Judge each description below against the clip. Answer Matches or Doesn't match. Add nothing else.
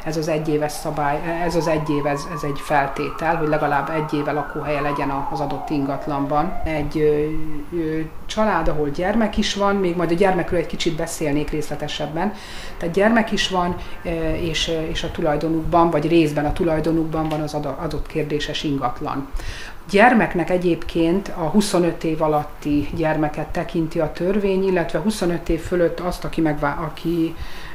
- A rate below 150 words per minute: Doesn't match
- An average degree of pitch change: Doesn't match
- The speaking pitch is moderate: Matches